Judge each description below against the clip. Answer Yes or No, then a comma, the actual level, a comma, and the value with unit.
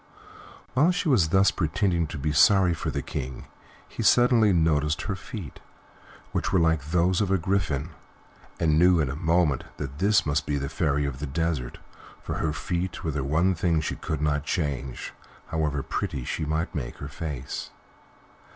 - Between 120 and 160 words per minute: No, average, 180 wpm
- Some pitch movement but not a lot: Yes, average, 3.8 semitones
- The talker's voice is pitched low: Yes, very low, 80 Hz